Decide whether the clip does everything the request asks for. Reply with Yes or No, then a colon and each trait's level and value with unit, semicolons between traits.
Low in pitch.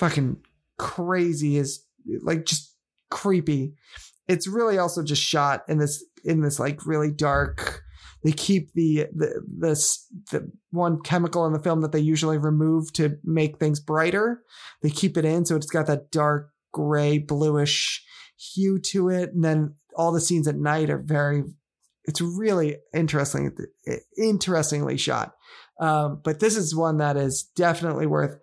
No: medium, 155 Hz